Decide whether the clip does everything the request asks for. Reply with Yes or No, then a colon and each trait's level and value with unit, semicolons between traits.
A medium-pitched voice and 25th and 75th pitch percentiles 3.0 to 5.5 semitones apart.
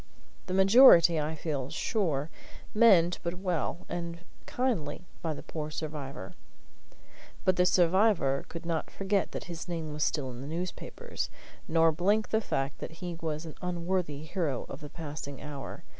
Yes: medium, 165 Hz; average, 3.4 semitones